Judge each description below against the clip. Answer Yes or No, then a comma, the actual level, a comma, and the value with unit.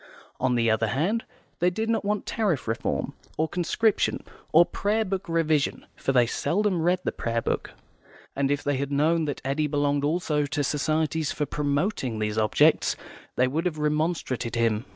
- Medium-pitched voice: Yes, medium, 150 Hz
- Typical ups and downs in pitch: Yes, average, 4.5 semitones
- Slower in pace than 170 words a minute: No, average, 175 wpm